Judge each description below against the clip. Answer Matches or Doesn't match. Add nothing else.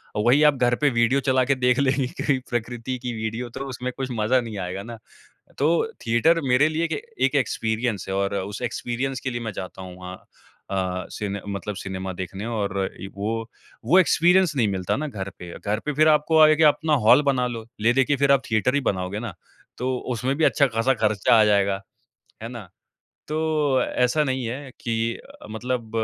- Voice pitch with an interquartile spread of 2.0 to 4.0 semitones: Doesn't match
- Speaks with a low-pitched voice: Matches